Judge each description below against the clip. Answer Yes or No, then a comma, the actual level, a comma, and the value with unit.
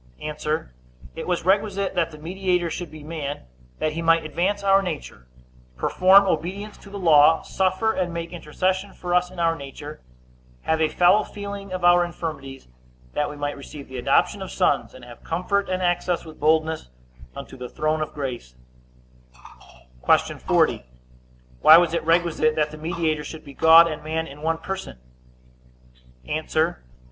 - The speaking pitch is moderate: Yes, medium, 165 Hz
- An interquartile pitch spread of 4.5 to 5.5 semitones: No, average, 3.2 semitones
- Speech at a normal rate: Yes, average, 165 wpm